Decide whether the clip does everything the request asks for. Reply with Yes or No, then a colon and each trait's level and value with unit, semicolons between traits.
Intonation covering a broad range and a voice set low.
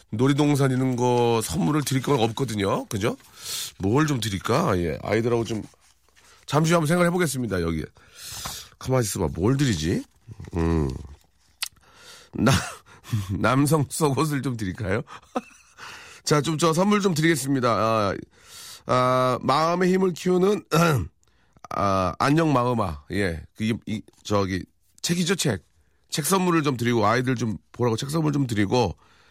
Yes: wide, 6.9 semitones; low, 125 Hz